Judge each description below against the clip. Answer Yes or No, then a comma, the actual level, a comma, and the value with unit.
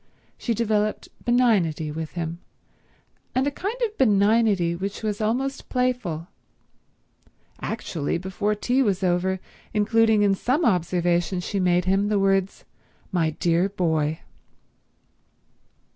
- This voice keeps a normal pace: No, slow, 115 wpm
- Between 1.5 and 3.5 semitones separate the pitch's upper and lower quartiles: No, average, 4.4 semitones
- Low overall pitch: No, high, 195 Hz